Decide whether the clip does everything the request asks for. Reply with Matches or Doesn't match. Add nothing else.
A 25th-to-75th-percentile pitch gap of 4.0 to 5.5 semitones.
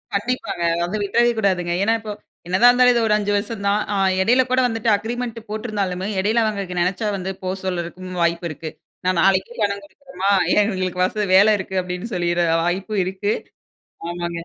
Doesn't match